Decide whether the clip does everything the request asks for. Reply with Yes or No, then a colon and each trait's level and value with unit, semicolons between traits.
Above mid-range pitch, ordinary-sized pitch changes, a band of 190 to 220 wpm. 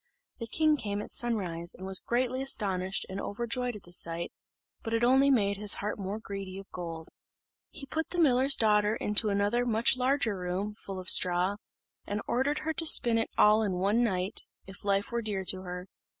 Yes: high, 210 Hz; average, 4.0 semitones; average, 200 wpm